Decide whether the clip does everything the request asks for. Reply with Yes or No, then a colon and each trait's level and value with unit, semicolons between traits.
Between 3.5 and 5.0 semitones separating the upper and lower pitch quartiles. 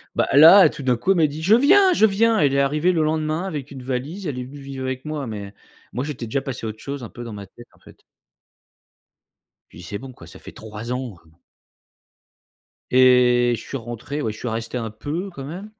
Yes: average, 4.5 semitones